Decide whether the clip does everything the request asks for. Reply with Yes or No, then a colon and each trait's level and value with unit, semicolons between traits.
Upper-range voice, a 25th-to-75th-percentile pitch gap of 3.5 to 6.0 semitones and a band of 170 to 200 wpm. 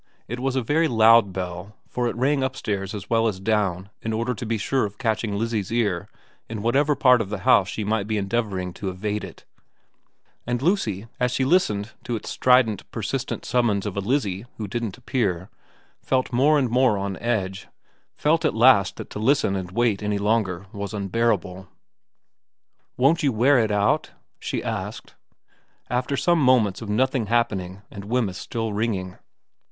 No: low, 110 Hz; average, 3.8 semitones; average, 180 wpm